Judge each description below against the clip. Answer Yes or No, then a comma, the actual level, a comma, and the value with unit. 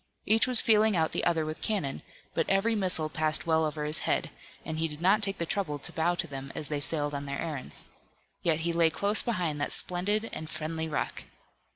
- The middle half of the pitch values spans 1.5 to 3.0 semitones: No, average, 4.1 semitones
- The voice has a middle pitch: Yes, medium, 160 Hz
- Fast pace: Yes, fast, 220 wpm